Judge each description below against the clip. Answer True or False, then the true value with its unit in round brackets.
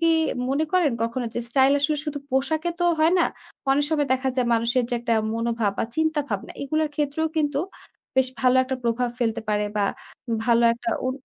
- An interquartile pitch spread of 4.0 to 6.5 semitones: True (4.3 semitones)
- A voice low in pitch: False (265 Hz)